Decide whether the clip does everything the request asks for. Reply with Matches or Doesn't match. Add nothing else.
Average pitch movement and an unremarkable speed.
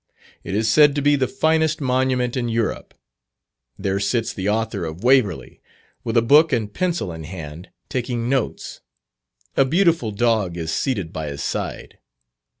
Doesn't match